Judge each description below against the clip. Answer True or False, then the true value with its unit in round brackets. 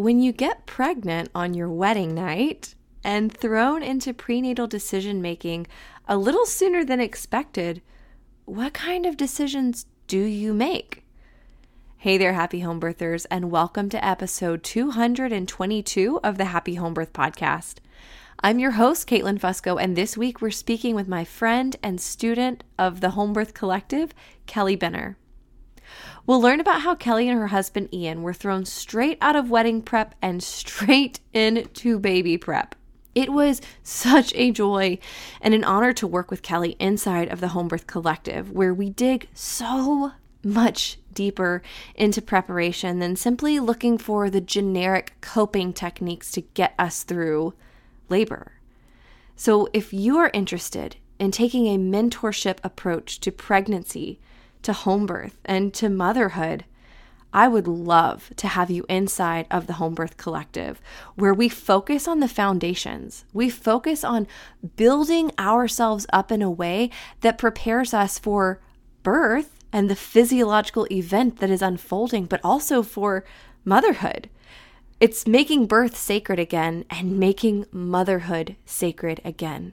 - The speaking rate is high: False (150 wpm)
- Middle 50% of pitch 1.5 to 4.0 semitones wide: False (4.7 semitones)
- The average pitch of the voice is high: True (205 Hz)